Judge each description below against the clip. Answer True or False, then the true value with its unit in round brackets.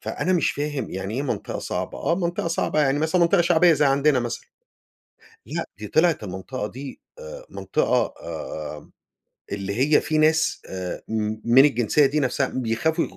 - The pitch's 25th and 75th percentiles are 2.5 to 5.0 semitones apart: False (5.6 semitones)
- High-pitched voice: False (140 Hz)